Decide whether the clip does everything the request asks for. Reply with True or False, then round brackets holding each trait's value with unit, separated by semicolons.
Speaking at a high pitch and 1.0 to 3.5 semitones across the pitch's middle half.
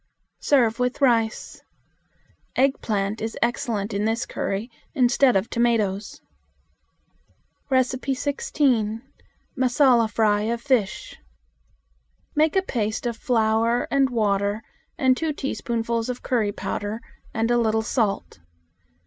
True (235 Hz; 3.0 semitones)